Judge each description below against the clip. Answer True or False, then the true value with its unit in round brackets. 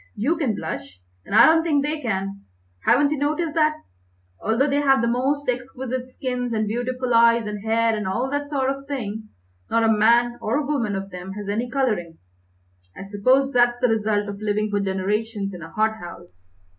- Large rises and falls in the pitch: False (4.6 semitones)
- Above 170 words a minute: True (190 wpm)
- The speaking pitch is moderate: False (230 Hz)